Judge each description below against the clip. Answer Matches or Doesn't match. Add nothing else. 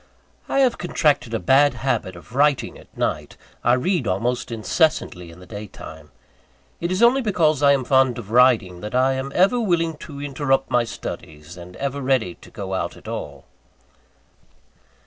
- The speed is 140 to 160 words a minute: Doesn't match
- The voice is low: Matches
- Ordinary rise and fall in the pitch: Doesn't match